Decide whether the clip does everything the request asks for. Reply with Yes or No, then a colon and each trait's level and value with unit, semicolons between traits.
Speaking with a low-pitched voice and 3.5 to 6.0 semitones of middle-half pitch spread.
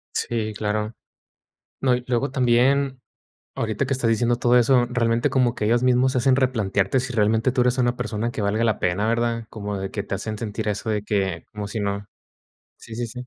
No: low, 115 Hz; average, 2.8 semitones